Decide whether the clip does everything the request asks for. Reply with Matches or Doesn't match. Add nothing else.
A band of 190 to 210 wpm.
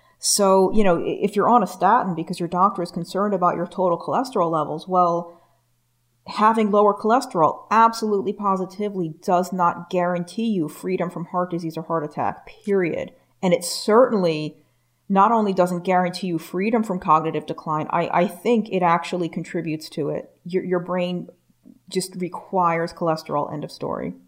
Doesn't match